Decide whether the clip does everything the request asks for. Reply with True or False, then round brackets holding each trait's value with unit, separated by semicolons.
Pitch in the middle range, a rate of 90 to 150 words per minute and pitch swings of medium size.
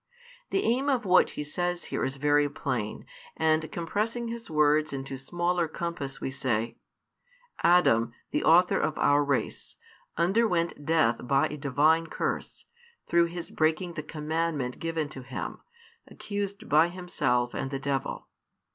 True (155 Hz; 145 wpm; 3.8 semitones)